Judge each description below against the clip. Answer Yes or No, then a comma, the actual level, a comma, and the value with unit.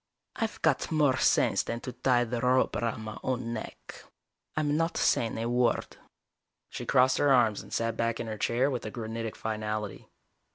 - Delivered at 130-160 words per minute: No, average, 180 wpm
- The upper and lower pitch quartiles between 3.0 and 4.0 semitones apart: No, narrow, 2.4 semitones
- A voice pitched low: Yes, low, 120 Hz